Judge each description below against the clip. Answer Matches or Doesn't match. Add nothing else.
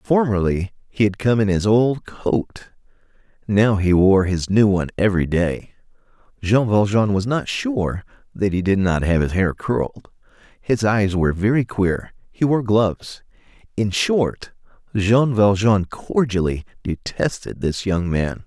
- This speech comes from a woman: Doesn't match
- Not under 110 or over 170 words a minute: Matches